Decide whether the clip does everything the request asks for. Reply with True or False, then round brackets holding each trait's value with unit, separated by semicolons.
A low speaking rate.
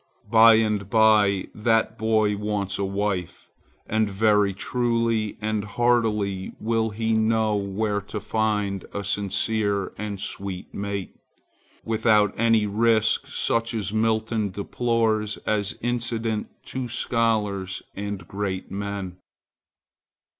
True (110 wpm)